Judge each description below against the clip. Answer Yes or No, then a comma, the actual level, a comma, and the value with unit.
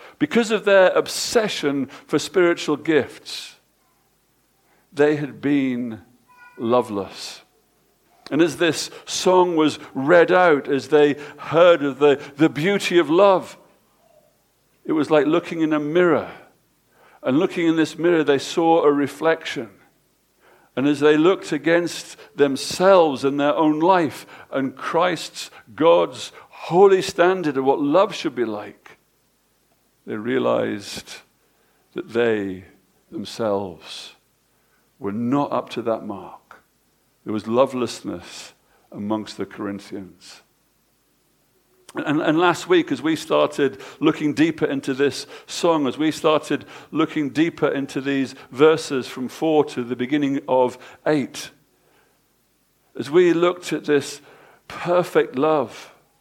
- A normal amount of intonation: Yes, average, 4.3 semitones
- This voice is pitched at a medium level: Yes, medium, 150 Hz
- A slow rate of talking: Yes, slow, 125 wpm